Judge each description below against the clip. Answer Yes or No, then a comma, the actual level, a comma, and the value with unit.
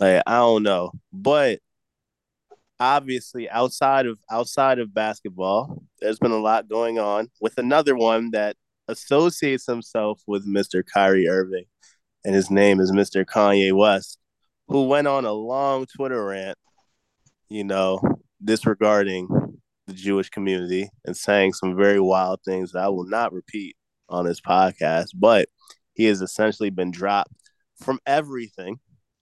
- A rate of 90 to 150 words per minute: Yes, average, 140 wpm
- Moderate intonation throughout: Yes, average, 3.9 semitones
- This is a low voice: Yes, low, 105 Hz